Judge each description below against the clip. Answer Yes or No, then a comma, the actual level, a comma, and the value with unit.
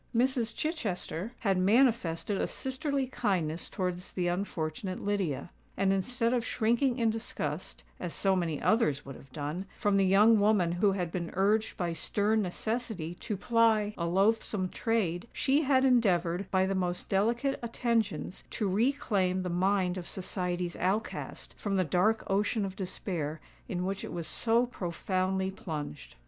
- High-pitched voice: Yes, high, 195 Hz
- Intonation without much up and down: No, average, 4.1 semitones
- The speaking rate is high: No, average, 155 wpm